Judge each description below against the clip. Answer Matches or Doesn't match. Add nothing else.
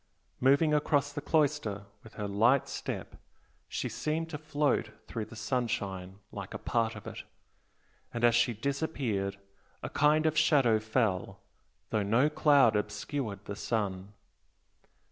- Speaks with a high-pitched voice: Doesn't match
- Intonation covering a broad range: Matches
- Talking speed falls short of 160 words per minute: Matches